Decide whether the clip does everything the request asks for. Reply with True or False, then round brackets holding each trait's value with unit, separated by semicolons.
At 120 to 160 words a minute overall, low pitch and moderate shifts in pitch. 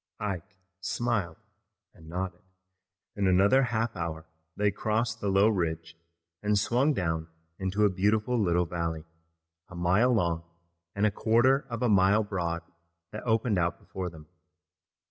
True (145 wpm; 100 Hz; 4.1 semitones)